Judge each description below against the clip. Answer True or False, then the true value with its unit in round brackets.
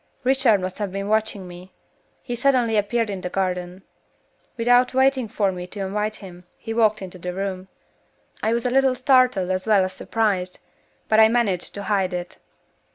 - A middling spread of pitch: True (3.9 semitones)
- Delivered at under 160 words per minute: False (180 wpm)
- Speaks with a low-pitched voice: False (205 Hz)